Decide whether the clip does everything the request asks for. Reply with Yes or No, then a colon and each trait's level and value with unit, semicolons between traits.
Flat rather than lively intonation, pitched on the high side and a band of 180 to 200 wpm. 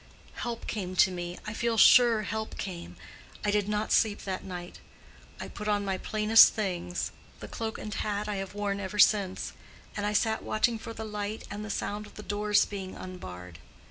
Yes: narrow, 2.2 semitones; high, 205 Hz; average, 190 wpm